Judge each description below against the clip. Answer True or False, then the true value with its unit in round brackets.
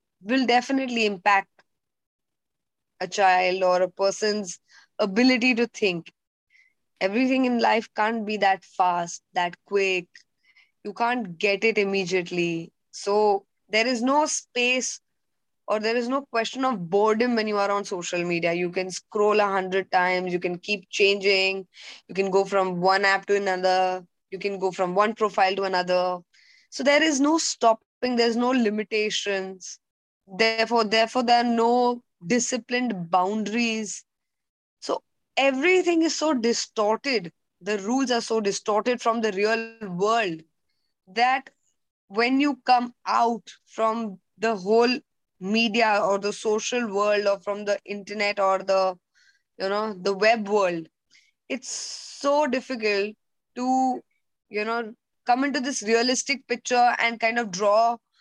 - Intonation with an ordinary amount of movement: True (3.8 semitones)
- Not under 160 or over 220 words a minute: False (140 wpm)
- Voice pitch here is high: True (215 Hz)